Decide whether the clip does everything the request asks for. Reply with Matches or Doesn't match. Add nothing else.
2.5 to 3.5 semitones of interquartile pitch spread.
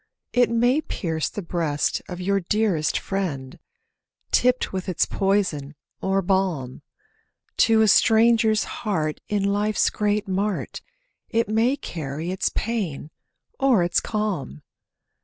Doesn't match